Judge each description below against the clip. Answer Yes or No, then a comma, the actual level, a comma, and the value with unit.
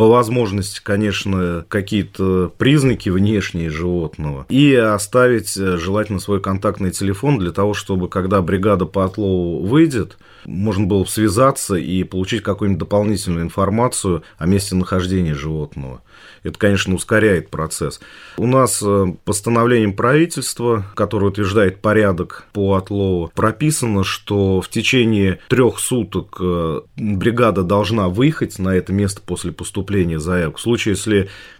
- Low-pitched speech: Yes, low, 100 Hz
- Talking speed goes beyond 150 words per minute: No, average, 125 wpm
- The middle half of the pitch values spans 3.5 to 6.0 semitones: No, average, 2.8 semitones